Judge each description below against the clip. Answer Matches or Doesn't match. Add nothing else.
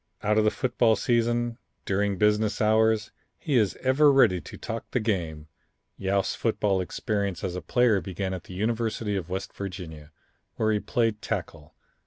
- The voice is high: Doesn't match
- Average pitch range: Matches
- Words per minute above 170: Doesn't match